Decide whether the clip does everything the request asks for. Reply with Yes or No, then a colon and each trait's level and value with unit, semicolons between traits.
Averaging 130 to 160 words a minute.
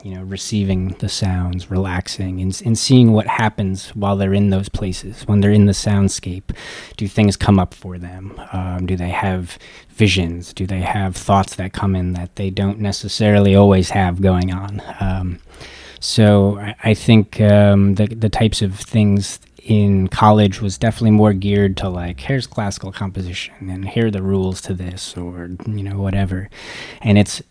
No: average, 180 wpm